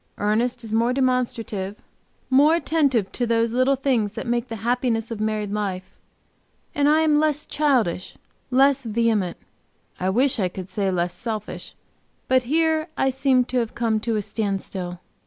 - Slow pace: No, average, 160 wpm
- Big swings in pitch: No, average, 4.0 semitones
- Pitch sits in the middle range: No, high, 235 Hz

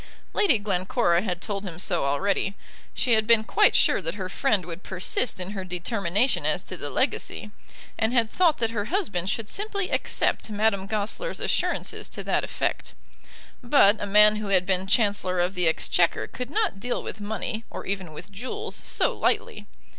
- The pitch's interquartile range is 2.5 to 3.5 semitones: No, average, 4.1 semitones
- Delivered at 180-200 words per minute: Yes, average, 185 wpm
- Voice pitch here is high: Yes, high, 205 Hz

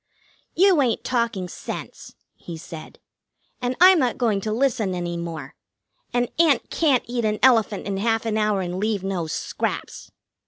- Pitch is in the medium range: No, high, 220 Hz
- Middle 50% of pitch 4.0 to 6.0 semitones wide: Yes, average, 4.8 semitones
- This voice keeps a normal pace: Yes, average, 160 wpm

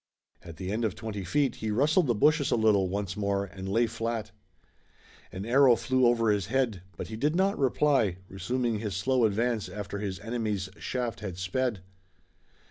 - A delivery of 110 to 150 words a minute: No, average, 180 wpm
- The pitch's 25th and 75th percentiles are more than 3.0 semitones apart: Yes, average, 4.1 semitones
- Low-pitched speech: Yes, low, 110 Hz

